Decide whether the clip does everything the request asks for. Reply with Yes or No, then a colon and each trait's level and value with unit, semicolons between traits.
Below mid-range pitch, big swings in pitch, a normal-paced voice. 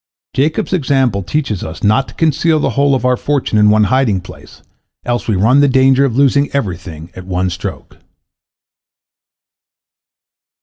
Yes: low, 125 Hz; wide, 5.8 semitones; average, 155 wpm